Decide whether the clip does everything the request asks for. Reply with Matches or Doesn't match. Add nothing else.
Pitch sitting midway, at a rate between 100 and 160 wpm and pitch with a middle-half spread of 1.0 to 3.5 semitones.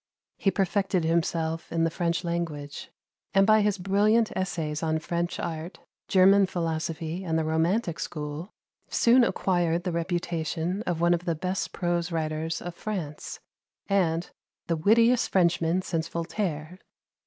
Matches